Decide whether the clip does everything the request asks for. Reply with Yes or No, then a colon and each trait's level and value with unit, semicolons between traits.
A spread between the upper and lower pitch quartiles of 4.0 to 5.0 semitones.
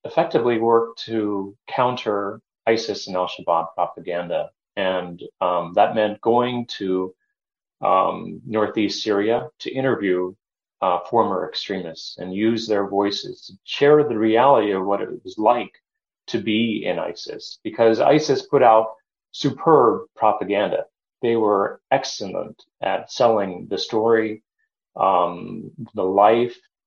No: average, 3.2 semitones